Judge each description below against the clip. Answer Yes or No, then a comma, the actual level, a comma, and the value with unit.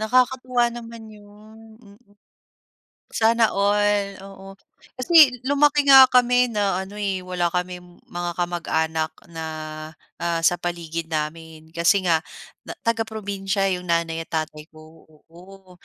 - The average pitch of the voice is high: Yes, high, 195 Hz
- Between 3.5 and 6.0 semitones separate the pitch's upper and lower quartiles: Yes, average, 4.8 semitones